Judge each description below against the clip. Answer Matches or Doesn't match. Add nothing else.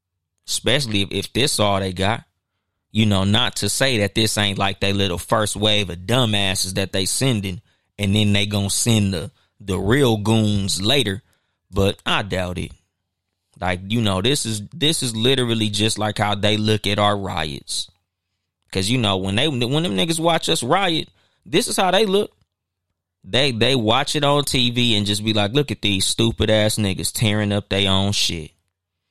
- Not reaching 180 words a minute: Doesn't match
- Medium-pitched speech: Doesn't match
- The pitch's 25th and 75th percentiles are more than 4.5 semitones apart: Doesn't match